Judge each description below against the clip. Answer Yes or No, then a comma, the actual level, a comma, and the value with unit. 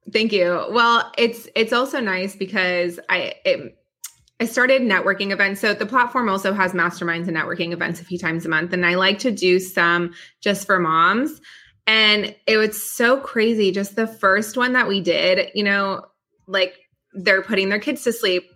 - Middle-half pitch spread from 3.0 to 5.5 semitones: Yes, average, 3.9 semitones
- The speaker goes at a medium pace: Yes, average, 190 wpm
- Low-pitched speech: No, high, 195 Hz